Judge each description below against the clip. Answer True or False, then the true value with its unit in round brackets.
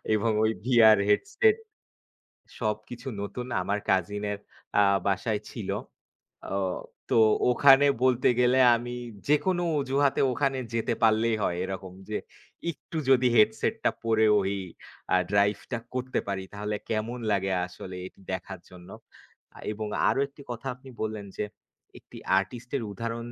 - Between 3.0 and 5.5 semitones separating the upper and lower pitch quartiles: True (3.7 semitones)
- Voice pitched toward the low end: True (110 Hz)